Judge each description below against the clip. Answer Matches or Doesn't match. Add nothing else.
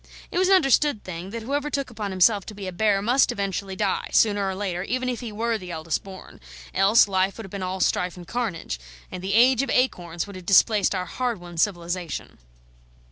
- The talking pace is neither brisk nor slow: Doesn't match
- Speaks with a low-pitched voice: Doesn't match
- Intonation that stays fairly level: Doesn't match